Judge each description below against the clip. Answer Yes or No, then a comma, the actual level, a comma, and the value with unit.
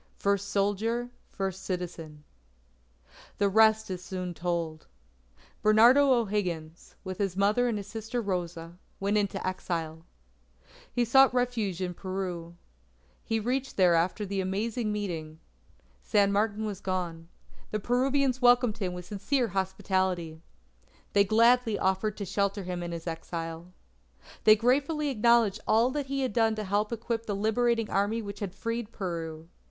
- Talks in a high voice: Yes, high, 200 Hz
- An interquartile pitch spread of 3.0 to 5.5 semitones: Yes, average, 4.1 semitones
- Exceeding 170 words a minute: No, average, 145 wpm